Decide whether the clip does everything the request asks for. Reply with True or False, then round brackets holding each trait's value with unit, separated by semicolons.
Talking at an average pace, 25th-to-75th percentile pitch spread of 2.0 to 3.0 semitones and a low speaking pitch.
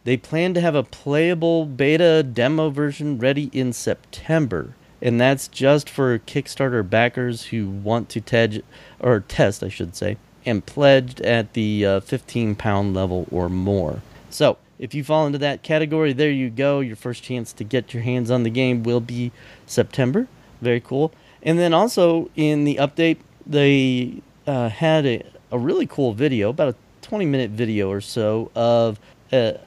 False (170 wpm; 4.2 semitones; 130 Hz)